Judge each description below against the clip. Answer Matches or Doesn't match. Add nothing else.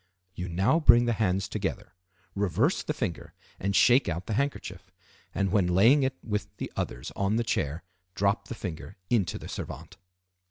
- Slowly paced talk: Doesn't match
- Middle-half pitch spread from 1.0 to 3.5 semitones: Doesn't match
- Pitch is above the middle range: Doesn't match